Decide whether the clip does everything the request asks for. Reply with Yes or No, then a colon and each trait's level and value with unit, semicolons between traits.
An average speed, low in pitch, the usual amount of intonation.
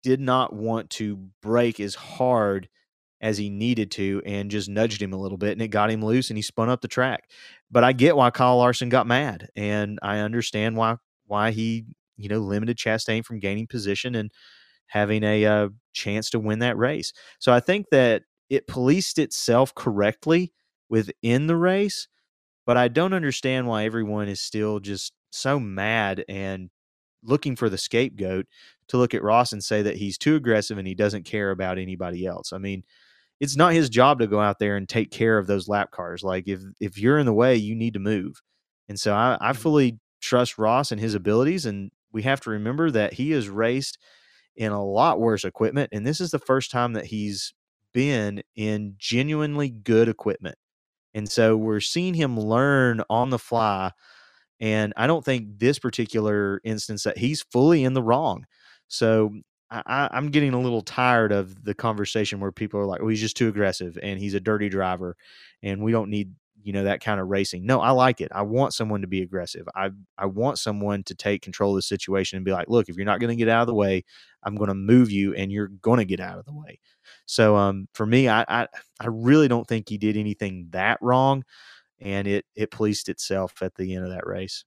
No: fast, 210 wpm; low, 110 Hz; average, 3.4 semitones